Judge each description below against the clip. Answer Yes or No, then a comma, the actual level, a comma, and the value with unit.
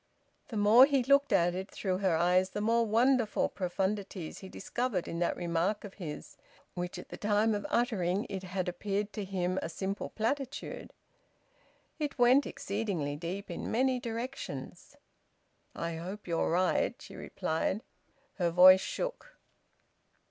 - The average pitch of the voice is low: No, high, 200 Hz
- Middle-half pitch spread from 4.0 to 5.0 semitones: Yes, average, 4.4 semitones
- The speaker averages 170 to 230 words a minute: No, average, 150 wpm